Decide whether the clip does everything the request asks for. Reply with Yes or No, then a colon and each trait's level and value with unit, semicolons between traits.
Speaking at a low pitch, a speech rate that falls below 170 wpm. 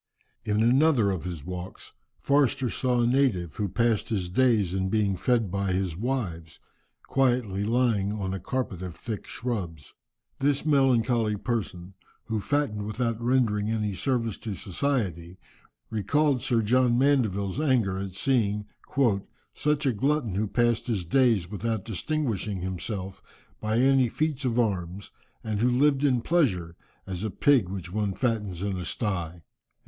Yes: low, 110 Hz; average, 150 wpm